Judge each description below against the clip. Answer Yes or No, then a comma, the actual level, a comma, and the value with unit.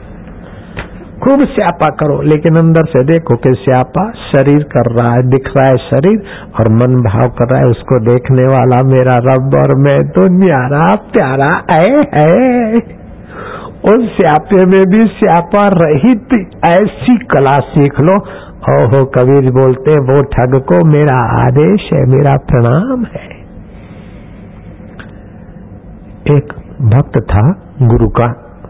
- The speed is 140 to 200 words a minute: No, average, 130 wpm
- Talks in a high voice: No, medium, 140 Hz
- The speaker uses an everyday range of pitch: No, wide, 6.7 semitones